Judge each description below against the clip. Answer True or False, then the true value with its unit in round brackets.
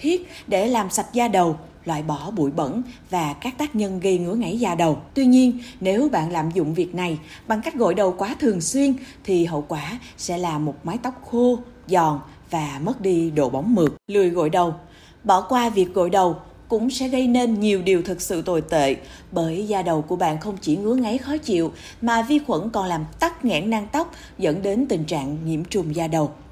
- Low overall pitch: False (190 Hz)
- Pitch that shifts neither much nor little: False (6.3 semitones)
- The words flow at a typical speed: True (215 wpm)